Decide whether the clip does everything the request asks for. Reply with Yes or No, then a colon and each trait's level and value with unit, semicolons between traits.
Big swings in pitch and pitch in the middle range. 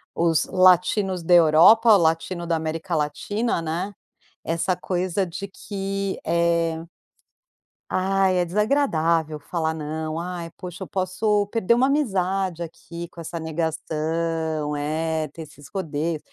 No: average, 3.0 semitones; medium, 170 Hz